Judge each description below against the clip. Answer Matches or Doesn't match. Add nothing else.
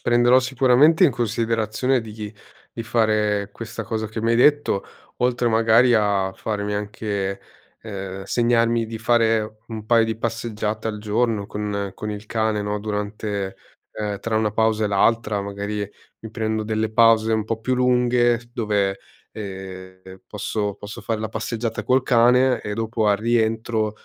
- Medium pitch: Doesn't match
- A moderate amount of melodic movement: Doesn't match